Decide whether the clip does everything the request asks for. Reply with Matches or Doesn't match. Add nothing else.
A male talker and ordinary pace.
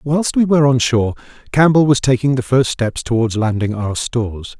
Matches